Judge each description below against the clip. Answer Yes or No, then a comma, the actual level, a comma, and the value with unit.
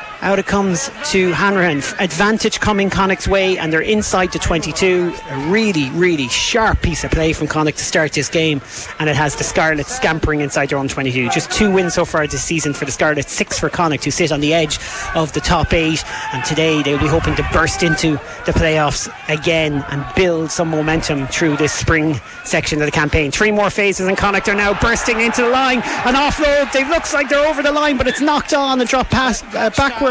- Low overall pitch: No, medium, 170 Hz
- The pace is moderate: No, fast, 220 wpm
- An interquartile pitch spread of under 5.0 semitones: No, wide, 5.6 semitones